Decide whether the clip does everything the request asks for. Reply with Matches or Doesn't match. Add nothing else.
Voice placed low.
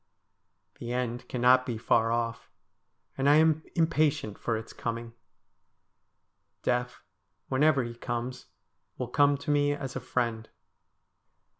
Matches